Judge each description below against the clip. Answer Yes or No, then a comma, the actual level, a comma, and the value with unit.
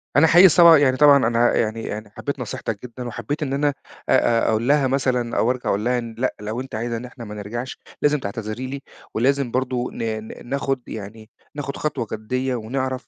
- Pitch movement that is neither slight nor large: Yes, average, 3.3 semitones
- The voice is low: Yes, low, 125 Hz